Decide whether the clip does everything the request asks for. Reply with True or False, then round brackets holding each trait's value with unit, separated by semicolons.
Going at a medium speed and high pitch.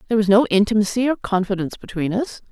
True (190 wpm; 210 Hz)